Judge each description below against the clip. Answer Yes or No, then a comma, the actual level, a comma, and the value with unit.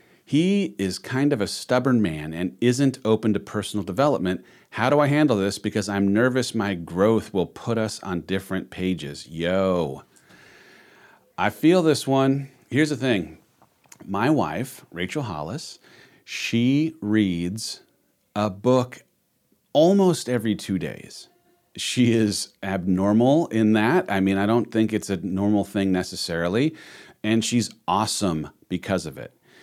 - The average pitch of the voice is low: Yes, low, 110 Hz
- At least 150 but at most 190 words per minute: No, average, 140 wpm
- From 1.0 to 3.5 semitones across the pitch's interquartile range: No, average, 4.6 semitones